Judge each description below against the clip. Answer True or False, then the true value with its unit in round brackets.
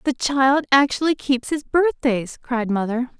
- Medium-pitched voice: False (265 Hz)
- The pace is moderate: True (150 wpm)